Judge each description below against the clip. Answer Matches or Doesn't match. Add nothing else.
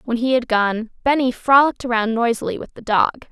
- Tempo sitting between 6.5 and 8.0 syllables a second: Doesn't match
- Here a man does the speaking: Doesn't match